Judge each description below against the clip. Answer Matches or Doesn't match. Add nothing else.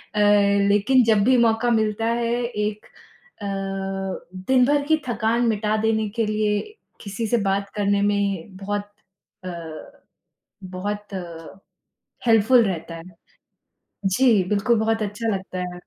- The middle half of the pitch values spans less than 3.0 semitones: Matches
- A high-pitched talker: Matches